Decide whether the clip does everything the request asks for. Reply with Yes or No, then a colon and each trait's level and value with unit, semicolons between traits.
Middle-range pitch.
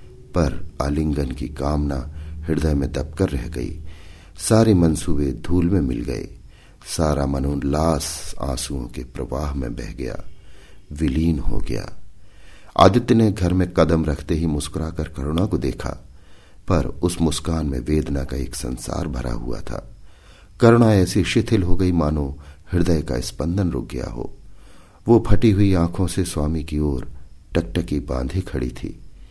No: very low, 80 Hz